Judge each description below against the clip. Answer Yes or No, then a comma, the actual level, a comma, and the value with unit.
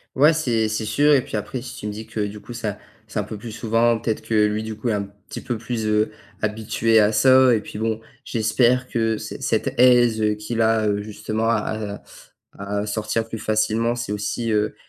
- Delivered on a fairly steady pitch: Yes, narrow, 1.6 semitones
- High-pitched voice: No, low, 110 Hz